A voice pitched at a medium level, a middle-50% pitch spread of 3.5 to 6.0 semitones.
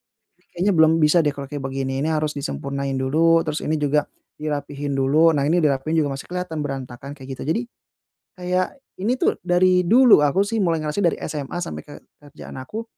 Yes: medium, 150 Hz; average, 4.1 semitones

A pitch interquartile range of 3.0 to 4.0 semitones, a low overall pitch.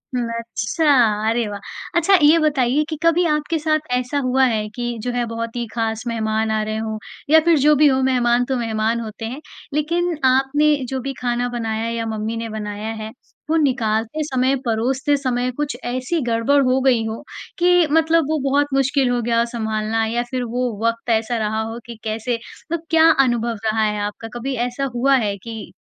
No: average, 3.6 semitones; high, 245 Hz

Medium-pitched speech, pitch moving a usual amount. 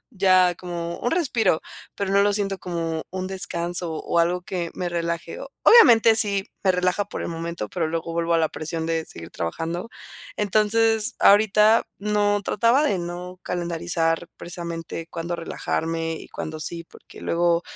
Yes: medium, 175 Hz; average, 3.3 semitones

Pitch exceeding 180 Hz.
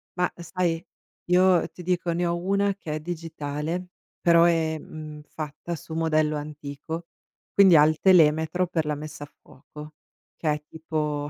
No: medium, 160 Hz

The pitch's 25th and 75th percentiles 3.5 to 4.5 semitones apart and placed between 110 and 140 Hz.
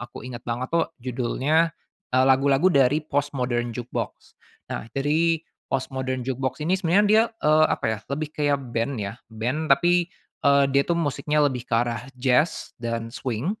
Yes: average, 3.8 semitones; low, 135 Hz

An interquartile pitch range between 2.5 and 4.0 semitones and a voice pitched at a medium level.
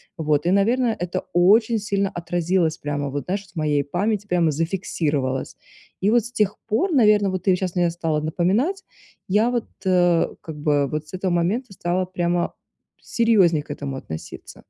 No: average, 4.6 semitones; medium, 180 Hz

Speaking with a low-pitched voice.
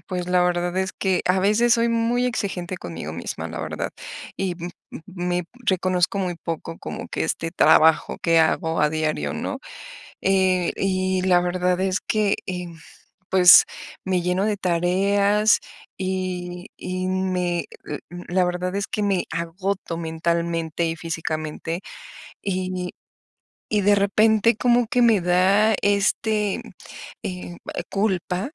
No: medium, 185 Hz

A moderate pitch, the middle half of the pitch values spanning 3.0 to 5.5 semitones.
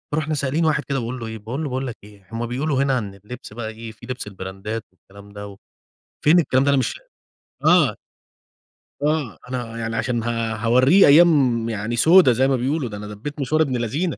No: low, 120 Hz; average, 4.1 semitones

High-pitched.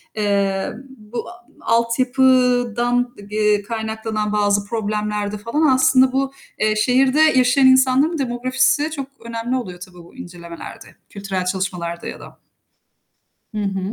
Yes: high, 230 Hz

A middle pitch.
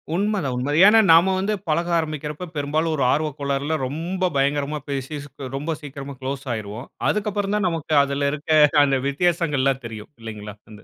Yes: medium, 145 Hz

